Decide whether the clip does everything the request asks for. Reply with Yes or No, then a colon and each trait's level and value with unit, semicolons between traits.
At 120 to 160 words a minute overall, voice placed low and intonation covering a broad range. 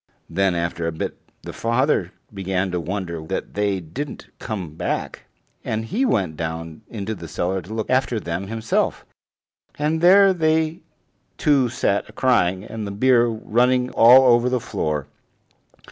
Yes: average, 150 wpm; low, 110 Hz; wide, 6.0 semitones